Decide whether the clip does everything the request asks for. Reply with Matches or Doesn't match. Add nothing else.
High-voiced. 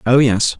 Doesn't match